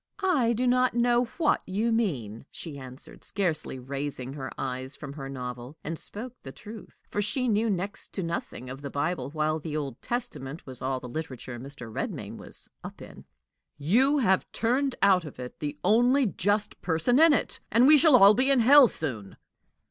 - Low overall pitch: No, medium, 170 Hz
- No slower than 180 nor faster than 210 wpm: Yes, average, 185 wpm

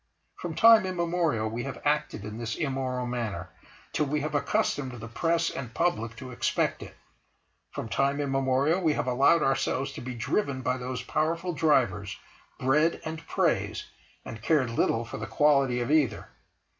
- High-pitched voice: No, low, 135 Hz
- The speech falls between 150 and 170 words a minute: Yes, average, 165 wpm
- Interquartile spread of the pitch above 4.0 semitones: Yes, average, 4.4 semitones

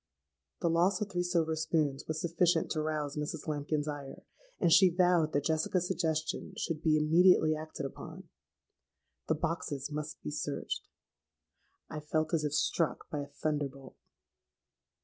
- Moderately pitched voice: Yes, medium, 155 Hz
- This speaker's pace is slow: No, average, 150 wpm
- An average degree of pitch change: No, narrow, 2.1 semitones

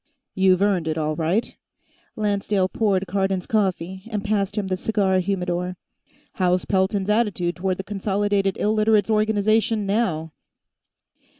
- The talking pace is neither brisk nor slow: No, slow, 125 wpm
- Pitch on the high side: Yes, high, 195 Hz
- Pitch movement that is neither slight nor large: No, narrow, 2.2 semitones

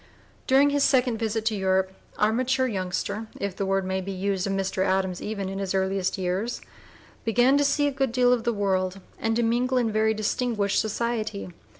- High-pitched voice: Yes, high, 215 Hz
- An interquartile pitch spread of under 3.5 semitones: No, average, 4.0 semitones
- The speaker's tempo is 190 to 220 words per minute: Yes, average, 200 wpm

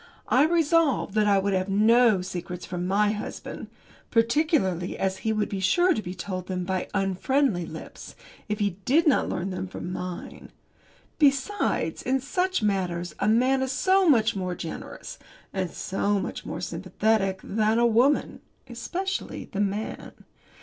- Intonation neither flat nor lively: No, wide, 5.8 semitones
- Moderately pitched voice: No, high, 210 Hz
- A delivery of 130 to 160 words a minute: Yes, average, 155 wpm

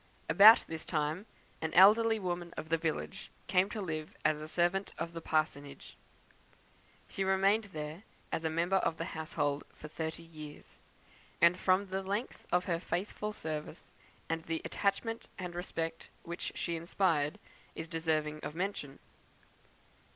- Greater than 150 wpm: No, average, 145 wpm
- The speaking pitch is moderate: Yes, medium, 170 Hz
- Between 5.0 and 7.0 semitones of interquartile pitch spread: No, average, 3.4 semitones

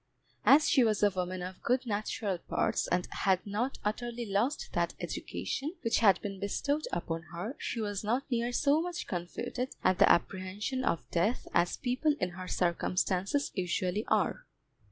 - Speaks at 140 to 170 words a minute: Yes, average, 165 wpm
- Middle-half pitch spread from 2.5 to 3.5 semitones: No, average, 5.3 semitones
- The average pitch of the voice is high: Yes, high, 210 Hz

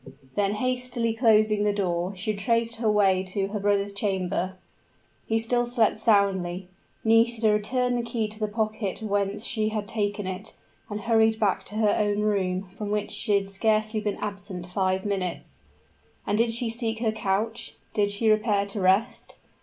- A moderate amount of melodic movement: No, narrow, 2.0 semitones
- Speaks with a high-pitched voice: Yes, high, 210 Hz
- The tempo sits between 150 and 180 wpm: Yes, average, 170 wpm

